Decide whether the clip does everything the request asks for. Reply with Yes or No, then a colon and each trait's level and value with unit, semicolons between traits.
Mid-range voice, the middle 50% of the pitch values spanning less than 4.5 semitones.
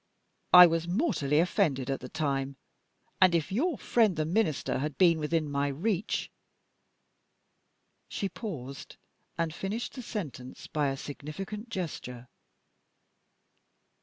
No: medium, 165 Hz; wide, 5.6 semitones